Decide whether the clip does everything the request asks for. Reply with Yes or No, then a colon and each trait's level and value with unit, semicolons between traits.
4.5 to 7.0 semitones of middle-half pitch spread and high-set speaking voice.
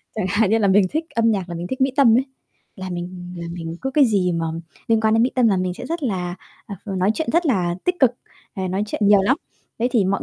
Yes: average, 5.0 semitones; high, 205 Hz